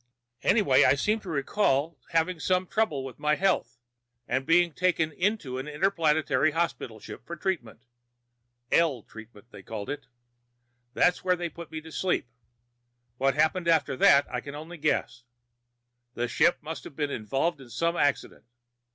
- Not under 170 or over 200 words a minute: No, average, 160 wpm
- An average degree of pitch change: Yes, average, 4.5 semitones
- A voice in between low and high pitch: Yes, medium, 155 Hz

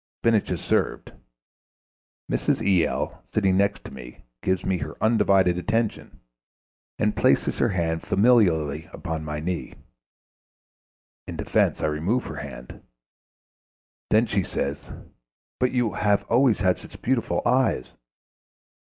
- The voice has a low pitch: Yes, very low, 95 Hz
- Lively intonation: Yes, wide, 5.8 semitones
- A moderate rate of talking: No, slow, 125 wpm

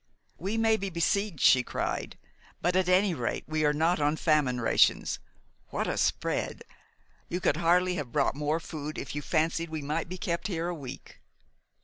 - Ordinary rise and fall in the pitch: Yes, average, 3.5 semitones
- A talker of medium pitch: Yes, medium, 165 Hz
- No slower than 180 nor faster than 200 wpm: Yes, average, 185 wpm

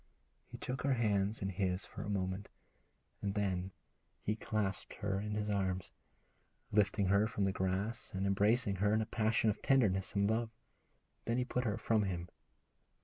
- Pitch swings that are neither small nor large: No, narrow, 2.2 semitones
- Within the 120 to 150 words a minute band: No, average, 175 wpm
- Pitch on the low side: Yes, low, 100 Hz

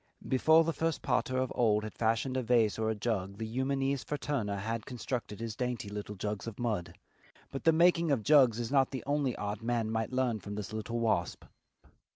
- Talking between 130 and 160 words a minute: No, average, 200 wpm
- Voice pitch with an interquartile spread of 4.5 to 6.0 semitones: No, average, 3.6 semitones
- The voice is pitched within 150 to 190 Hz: No, low, 115 Hz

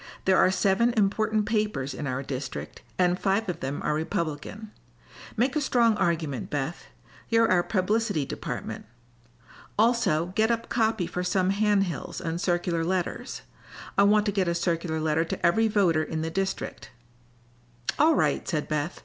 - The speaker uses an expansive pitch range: No, average, 4.8 semitones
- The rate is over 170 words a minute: No, average, 160 wpm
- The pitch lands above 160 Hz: Yes, medium, 185 Hz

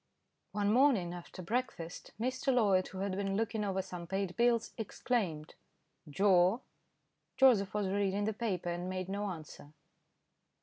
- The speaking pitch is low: No, high, 195 Hz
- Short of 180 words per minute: Yes, average, 140 wpm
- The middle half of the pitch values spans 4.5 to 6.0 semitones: No, average, 3.5 semitones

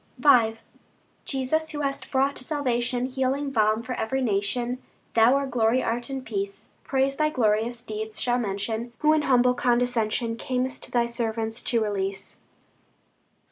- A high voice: Yes, high, 245 Hz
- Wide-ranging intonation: No, average, 3.0 semitones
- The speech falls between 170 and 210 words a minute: No, average, 140 wpm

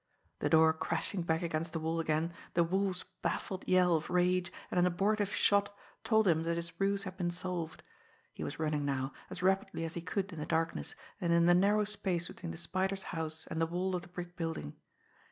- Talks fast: Yes, fast, 210 wpm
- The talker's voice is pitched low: No, medium, 175 Hz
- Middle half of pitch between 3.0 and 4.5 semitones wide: No, narrow, 2.5 semitones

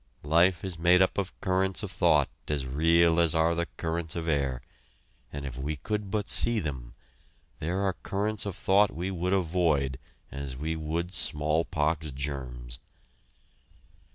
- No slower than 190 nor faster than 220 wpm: No, average, 155 wpm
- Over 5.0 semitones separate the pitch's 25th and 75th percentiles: No, average, 4.3 semitones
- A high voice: No, very low, 80 Hz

